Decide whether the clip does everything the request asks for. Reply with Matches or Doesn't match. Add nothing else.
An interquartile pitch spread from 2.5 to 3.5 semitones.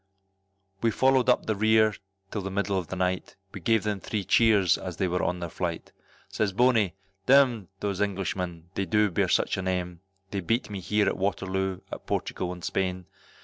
Matches